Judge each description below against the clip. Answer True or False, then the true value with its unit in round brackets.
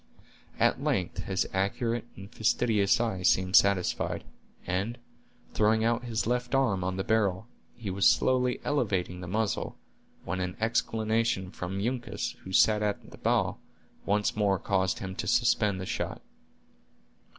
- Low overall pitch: True (105 Hz)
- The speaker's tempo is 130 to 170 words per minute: True (145 wpm)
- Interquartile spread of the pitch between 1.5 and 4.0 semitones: True (3.5 semitones)